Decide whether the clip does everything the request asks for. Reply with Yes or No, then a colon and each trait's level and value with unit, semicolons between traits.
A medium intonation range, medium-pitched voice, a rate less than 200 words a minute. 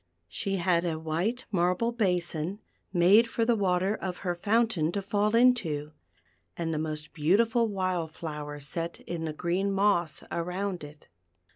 Yes: average, 4.0 semitones; medium, 180 Hz; average, 150 wpm